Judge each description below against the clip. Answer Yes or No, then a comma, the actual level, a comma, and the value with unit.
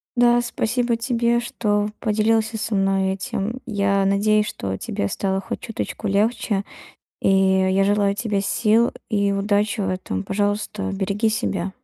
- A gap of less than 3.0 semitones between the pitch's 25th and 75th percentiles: Yes, narrow, 2.4 semitones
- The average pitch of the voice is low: No, high, 205 Hz